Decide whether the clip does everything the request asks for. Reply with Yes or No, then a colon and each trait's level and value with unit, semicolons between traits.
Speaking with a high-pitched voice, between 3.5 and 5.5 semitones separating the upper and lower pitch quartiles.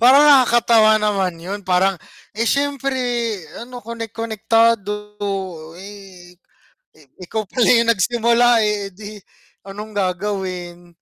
No: high, 210 Hz; average, 3.1 semitones